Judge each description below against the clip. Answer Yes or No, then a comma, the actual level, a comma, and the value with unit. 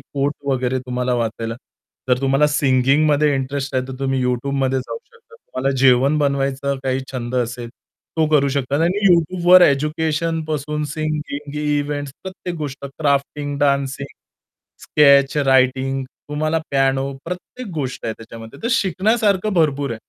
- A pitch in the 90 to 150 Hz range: Yes, medium, 140 Hz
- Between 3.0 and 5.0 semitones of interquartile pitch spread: No, narrow, 2.6 semitones